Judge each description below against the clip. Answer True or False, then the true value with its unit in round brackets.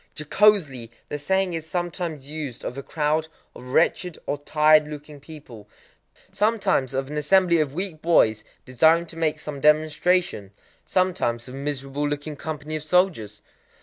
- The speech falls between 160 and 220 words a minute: False (145 wpm)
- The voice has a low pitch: False (150 Hz)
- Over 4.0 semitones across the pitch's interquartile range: False (3.6 semitones)